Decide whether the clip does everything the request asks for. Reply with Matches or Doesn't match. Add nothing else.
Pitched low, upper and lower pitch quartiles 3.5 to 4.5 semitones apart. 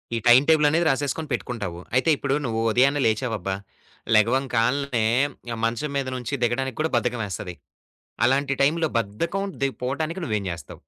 Matches